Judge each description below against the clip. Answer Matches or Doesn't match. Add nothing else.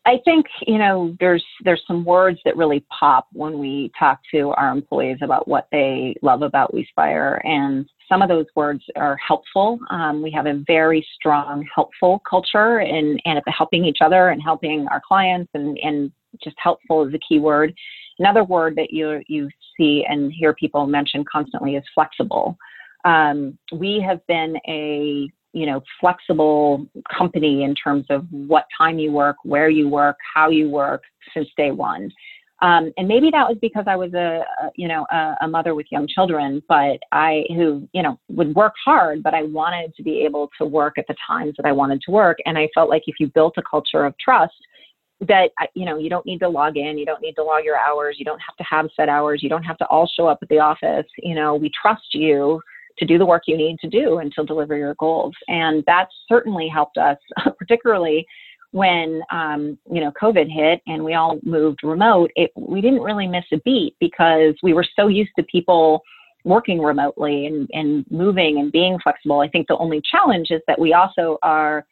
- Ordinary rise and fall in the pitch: Matches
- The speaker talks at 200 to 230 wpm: Matches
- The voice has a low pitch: Doesn't match